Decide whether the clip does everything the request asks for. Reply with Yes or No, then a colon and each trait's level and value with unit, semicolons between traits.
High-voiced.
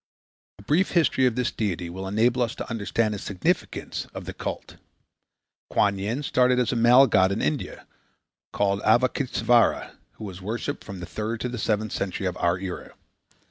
No: low, 110 Hz